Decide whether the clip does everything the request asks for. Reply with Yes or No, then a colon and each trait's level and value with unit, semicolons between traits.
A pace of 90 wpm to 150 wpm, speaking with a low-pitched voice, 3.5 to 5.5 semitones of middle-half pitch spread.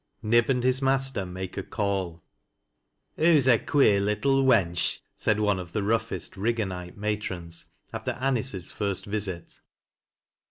Yes: slow, 135 wpm; low, 105 Hz; average, 5.0 semitones